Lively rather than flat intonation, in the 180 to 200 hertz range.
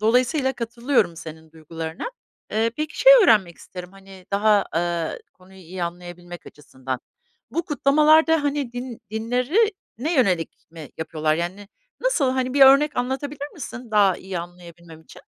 No: wide, 7.7 semitones; high, 210 Hz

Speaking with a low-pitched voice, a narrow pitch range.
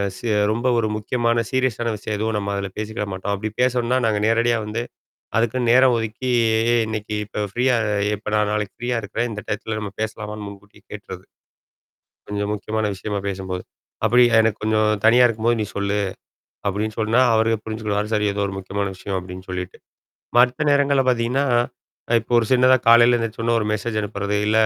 Yes: low, 110 Hz; narrow, 2.3 semitones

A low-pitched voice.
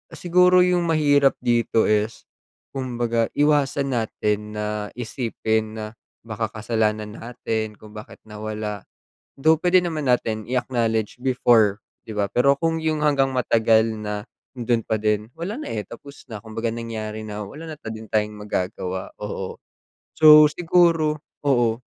Yes: low, 115 Hz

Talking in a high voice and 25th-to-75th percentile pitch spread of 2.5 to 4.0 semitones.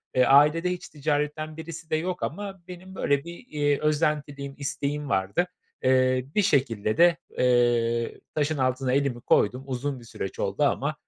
No: medium, 145 Hz; average, 3.6 semitones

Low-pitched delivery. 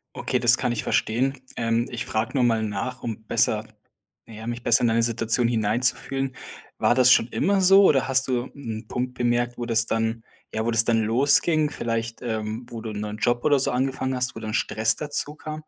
Yes: low, 120 Hz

